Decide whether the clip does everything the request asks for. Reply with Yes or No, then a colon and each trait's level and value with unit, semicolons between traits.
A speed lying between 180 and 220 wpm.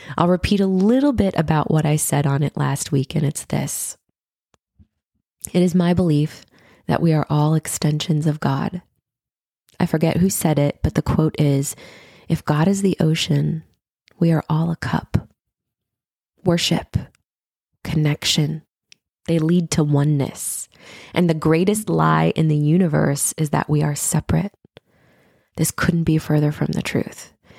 No: average, 155 wpm